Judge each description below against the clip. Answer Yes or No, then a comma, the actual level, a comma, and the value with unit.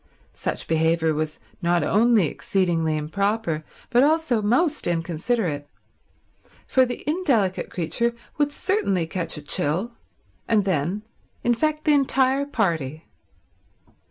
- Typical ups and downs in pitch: No, wide, 7.6 semitones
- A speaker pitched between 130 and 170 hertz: No, high, 200 Hz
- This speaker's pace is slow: Yes, slow, 110 wpm